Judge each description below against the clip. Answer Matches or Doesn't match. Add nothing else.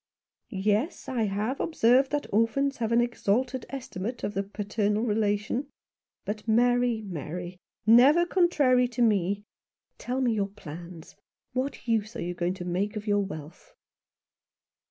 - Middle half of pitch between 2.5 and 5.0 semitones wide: Matches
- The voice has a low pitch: Doesn't match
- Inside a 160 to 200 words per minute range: Doesn't match